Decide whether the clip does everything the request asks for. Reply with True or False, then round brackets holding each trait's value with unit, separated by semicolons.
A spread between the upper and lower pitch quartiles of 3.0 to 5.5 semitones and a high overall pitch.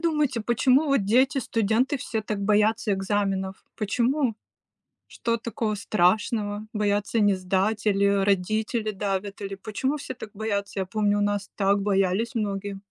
False (2.5 semitones; 210 Hz)